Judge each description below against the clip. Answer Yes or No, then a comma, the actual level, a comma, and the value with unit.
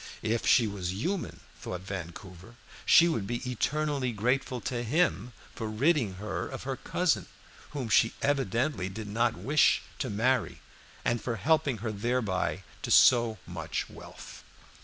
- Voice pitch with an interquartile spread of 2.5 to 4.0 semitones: No, average, 4.7 semitones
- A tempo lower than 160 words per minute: Yes, average, 145 wpm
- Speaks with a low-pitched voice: Yes, low, 115 Hz